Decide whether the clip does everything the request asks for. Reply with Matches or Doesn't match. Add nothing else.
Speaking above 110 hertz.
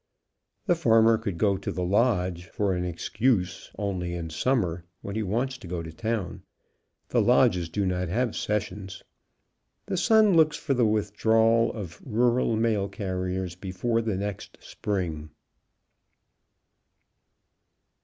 Doesn't match